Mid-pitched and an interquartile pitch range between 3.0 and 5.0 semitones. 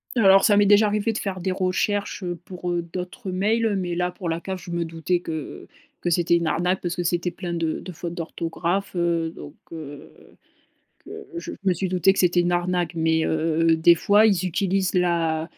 No: medium, 175 Hz; narrow, 2.4 semitones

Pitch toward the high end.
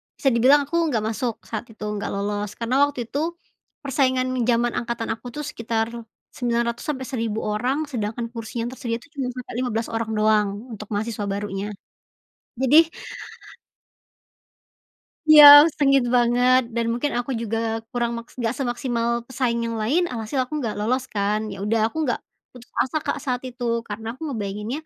Yes: high, 235 Hz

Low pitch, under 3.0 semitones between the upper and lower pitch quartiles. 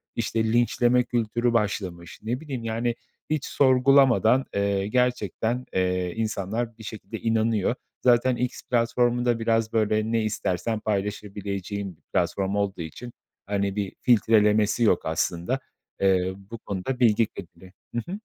No: low, 110 Hz; average, 3.3 semitones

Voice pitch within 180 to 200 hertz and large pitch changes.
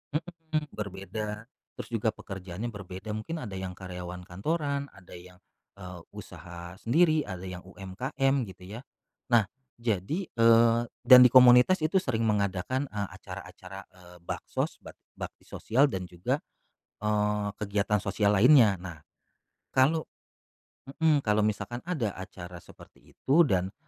No: low, 105 Hz; wide, 5.7 semitones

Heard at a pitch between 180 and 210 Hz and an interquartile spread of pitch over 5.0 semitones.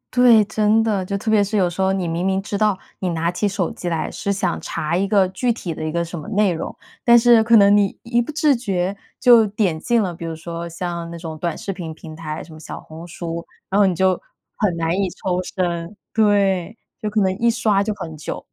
No: high, 190 Hz; average, 3.8 semitones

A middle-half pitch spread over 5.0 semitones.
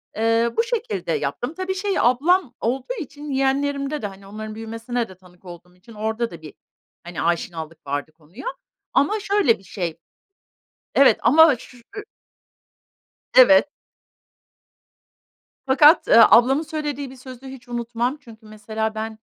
Yes: wide, 5.6 semitones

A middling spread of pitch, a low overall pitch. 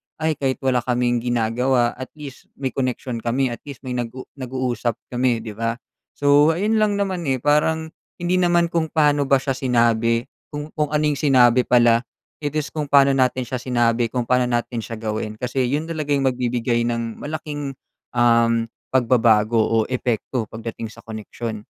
Yes: average, 3.6 semitones; low, 125 Hz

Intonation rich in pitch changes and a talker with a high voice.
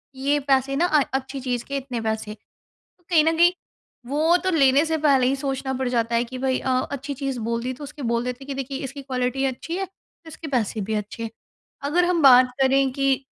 No: narrow, 2.4 semitones; very high, 270 Hz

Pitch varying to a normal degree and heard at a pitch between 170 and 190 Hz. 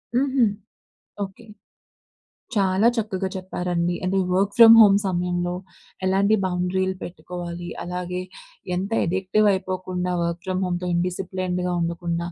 No: narrow, 1.5 semitones; medium, 185 Hz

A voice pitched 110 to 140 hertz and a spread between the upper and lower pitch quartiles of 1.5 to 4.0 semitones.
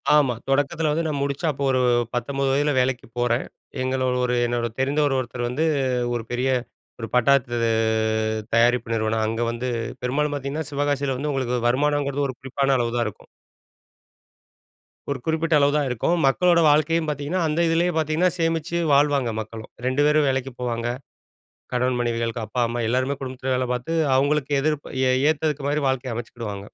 Yes: low, 135 Hz; average, 3.3 semitones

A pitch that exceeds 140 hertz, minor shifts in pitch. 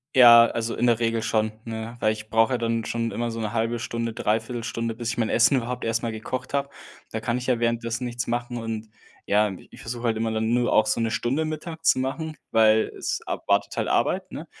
No: low, 115 Hz; narrow, 1.4 semitones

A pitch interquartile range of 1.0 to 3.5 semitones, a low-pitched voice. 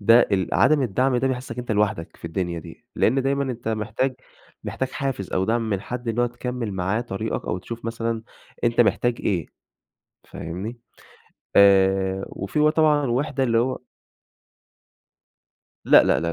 No: average, 4.5 semitones; low, 115 Hz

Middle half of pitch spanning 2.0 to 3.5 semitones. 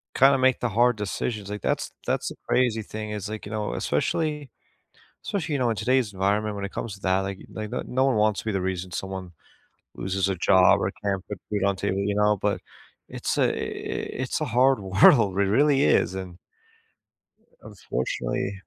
No: average, 4.0 semitones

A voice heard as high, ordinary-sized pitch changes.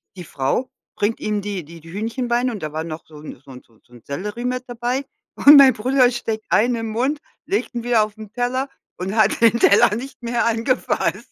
Yes: high, 225 Hz; average, 4.1 semitones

